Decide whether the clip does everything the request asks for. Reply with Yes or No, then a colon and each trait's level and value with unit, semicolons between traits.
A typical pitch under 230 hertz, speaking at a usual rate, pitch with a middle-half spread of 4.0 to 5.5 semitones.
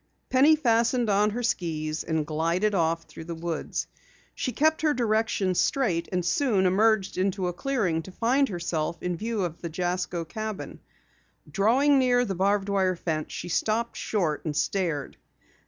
Yes: high, 190 Hz; average, 160 wpm; average, 5.2 semitones